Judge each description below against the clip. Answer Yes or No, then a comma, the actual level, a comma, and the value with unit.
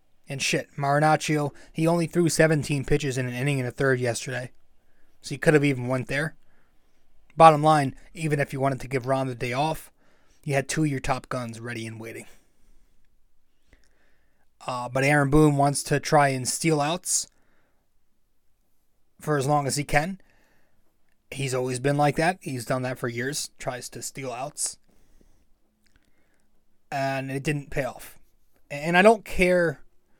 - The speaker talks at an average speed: Yes, average, 165 wpm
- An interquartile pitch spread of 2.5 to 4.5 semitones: Yes, average, 2.9 semitones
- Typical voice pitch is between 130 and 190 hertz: Yes, medium, 140 Hz